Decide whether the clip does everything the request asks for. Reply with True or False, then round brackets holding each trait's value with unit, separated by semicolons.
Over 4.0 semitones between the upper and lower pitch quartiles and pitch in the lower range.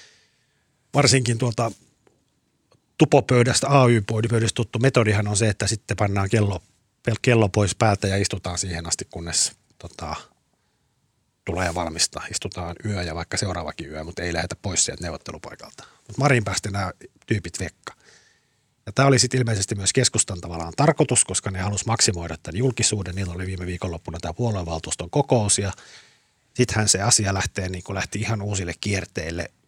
True (4.4 semitones; 105 Hz)